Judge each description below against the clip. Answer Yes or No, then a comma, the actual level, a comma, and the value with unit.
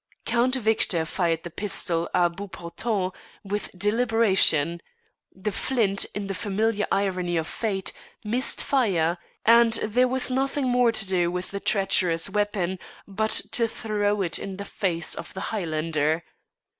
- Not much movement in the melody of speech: No, average, 4.2 semitones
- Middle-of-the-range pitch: No, high, 200 Hz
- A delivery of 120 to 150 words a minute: Yes, average, 145 wpm